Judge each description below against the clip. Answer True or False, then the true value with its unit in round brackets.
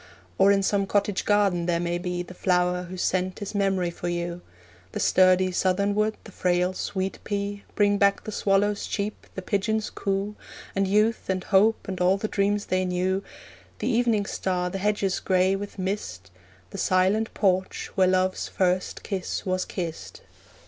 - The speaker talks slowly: False (170 wpm)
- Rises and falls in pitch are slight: True (1.9 semitones)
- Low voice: False (190 Hz)